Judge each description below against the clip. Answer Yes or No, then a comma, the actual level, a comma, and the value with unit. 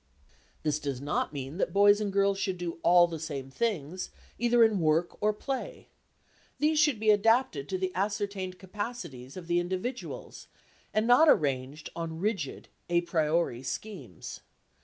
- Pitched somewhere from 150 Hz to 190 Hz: Yes, medium, 185 Hz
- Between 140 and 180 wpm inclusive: Yes, average, 155 wpm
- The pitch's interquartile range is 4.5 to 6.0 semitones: Yes, wide, 5.5 semitones